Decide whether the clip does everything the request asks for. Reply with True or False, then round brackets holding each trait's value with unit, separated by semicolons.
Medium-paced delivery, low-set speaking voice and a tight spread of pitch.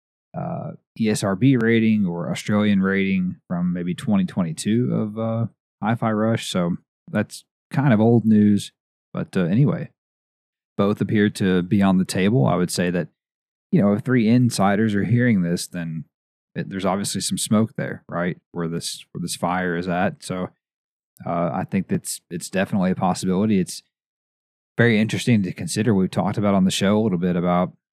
False (170 wpm; 105 Hz; 3.7 semitones)